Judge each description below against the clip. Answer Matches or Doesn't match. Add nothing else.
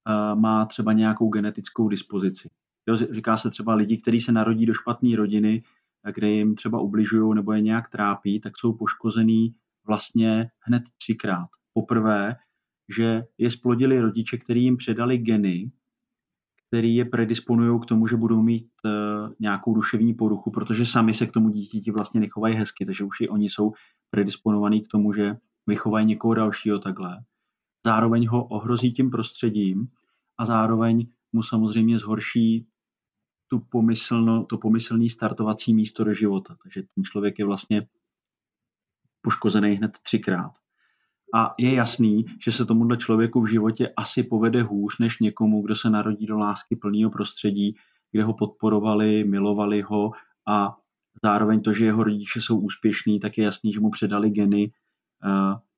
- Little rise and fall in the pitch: Matches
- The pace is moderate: Matches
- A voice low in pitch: Matches